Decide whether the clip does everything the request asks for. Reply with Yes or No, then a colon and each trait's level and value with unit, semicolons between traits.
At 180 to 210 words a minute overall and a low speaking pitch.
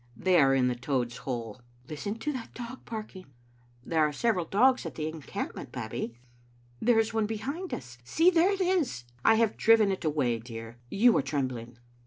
No: fast, 205 wpm; medium, 155 Hz